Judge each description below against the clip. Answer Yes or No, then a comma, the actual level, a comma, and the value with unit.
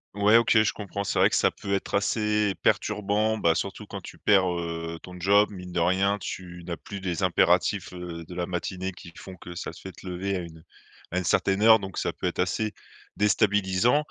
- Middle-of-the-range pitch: No, very low, 95 Hz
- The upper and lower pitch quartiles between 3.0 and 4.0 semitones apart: No, narrow, 2.6 semitones